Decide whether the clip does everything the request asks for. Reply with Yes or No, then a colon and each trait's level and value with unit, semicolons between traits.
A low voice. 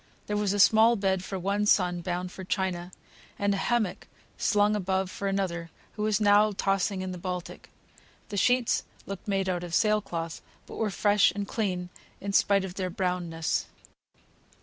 No: high, 195 Hz